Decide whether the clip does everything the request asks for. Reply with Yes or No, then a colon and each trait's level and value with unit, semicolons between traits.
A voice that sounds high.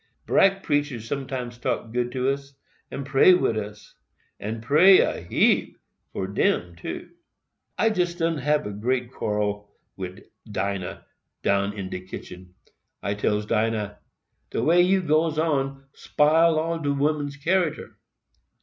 No: low, 135 Hz